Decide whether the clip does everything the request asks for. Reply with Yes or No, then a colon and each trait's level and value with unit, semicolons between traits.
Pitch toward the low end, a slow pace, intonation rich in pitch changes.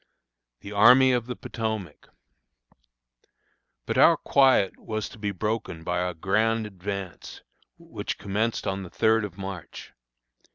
No: low, 105 Hz; slow, 130 wpm; average, 2.8 semitones